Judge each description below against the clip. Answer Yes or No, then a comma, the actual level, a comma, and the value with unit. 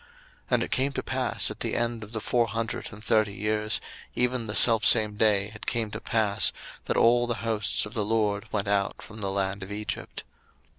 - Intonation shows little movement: Yes, narrow, 1.9 semitones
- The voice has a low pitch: Yes, low, 110 Hz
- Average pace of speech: No, fast, 210 wpm